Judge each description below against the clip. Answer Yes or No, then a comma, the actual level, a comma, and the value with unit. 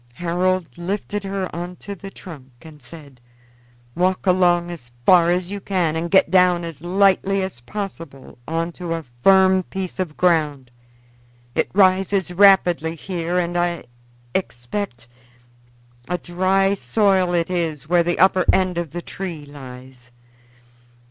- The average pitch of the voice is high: No, medium, 175 Hz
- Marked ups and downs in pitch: No, narrow, 2.5 semitones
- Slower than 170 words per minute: Yes, average, 140 wpm